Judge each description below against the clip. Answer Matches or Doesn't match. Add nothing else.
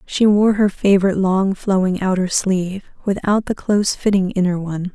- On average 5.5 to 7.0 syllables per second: Doesn't match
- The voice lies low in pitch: Doesn't match